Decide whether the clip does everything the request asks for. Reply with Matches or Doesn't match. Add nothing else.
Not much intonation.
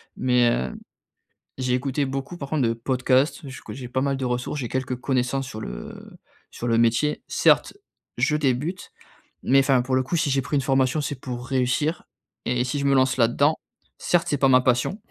Matches